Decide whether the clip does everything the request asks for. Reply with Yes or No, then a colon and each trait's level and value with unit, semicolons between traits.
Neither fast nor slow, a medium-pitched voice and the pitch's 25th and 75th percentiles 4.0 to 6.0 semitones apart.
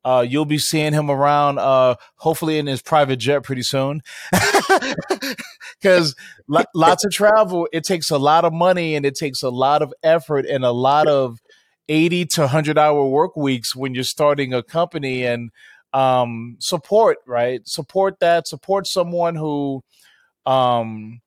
Yes: average, 160 wpm; medium, 150 Hz; average, 4.3 semitones